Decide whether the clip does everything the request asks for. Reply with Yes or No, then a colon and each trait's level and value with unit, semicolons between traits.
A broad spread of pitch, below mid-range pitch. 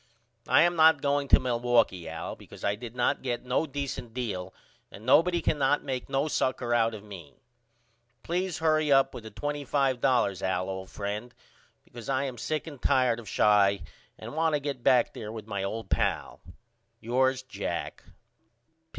No: average, 4.7 semitones; low, 125 Hz